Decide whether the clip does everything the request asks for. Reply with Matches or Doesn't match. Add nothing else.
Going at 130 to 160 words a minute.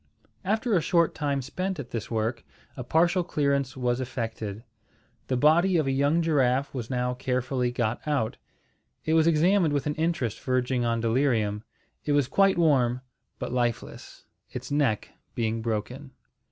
Matches